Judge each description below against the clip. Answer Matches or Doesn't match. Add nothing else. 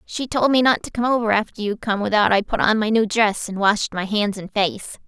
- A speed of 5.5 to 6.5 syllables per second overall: Doesn't match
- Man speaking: Doesn't match